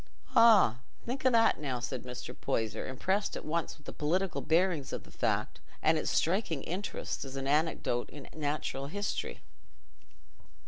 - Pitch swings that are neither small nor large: No, wide, 6.0 semitones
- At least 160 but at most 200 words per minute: Yes, average, 165 wpm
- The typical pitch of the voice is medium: Yes, medium, 155 Hz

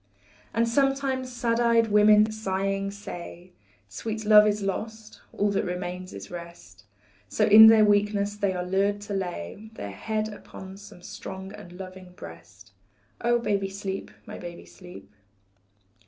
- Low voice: No, high, 200 Hz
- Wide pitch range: No, average, 3.1 semitones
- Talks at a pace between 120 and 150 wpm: Yes, average, 145 wpm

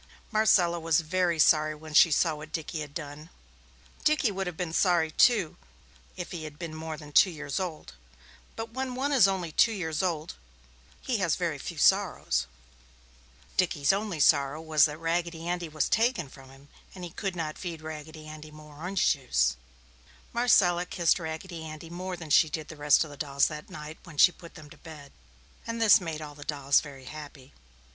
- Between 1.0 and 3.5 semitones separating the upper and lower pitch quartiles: Yes, average, 2.8 semitones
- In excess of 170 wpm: Yes, average, 190 wpm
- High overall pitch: No, medium, 160 Hz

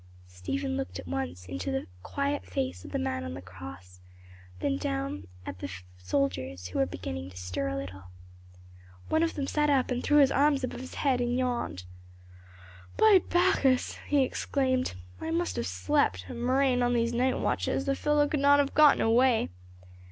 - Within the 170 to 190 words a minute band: Yes, average, 180 wpm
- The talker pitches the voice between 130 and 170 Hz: Yes, medium, 140 Hz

